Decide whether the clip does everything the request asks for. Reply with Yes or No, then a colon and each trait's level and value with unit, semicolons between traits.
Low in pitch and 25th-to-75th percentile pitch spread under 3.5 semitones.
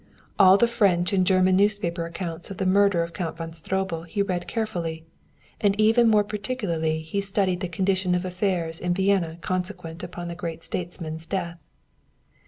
No: medium, 185 Hz; average, 2.8 semitones